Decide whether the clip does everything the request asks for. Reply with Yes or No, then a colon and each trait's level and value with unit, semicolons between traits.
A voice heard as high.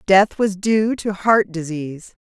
Yes: high, 195 Hz